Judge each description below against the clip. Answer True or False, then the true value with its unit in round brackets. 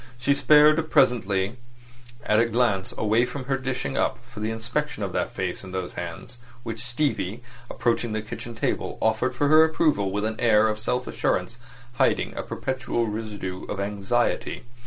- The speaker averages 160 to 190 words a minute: True (165 wpm)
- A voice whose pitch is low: True (115 Hz)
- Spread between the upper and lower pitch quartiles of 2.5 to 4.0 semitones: True (3.3 semitones)